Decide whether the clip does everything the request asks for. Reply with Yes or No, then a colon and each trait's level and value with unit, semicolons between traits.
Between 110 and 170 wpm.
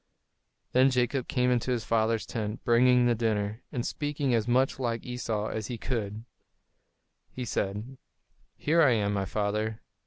Yes: average, 155 wpm